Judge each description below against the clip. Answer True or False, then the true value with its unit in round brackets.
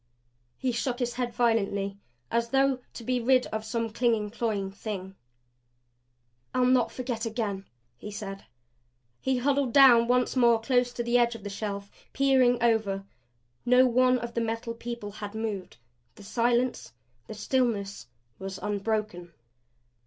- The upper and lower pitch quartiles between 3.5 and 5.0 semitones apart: False (3.1 semitones)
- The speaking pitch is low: False (230 Hz)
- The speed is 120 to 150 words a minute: True (145 wpm)